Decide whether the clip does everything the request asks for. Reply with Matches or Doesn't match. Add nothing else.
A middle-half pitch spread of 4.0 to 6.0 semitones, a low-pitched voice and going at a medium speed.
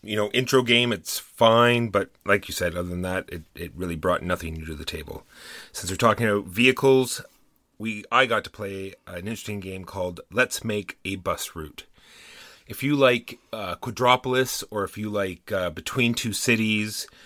Matches